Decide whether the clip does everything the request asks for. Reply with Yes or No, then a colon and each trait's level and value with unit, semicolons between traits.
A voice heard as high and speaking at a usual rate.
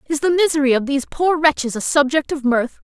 No: very high, 290 Hz; fast, 225 wpm